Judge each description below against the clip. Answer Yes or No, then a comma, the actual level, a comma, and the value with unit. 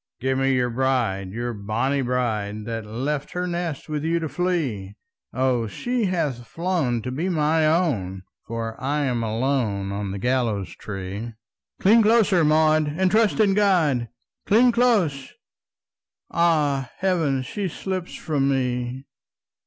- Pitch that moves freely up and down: Yes, wide, 6.6 semitones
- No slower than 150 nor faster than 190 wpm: No, slow, 135 wpm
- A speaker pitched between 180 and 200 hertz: No, low, 135 Hz